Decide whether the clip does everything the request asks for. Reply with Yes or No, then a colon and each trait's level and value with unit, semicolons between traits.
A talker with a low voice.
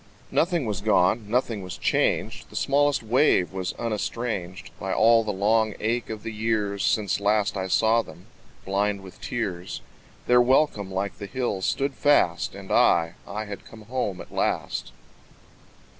Yes: low, 105 Hz